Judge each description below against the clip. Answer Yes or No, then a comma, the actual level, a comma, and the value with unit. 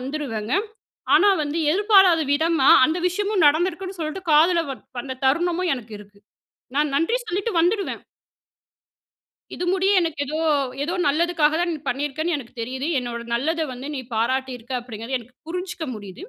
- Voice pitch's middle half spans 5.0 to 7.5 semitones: Yes, average, 5.3 semitones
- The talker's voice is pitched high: Yes, very high, 305 Hz